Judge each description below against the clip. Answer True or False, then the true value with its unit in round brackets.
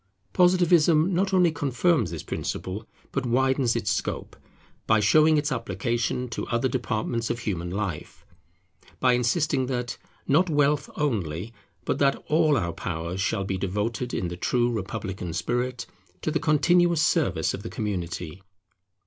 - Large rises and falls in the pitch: True (7.1 semitones)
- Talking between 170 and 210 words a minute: False (145 wpm)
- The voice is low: True (120 Hz)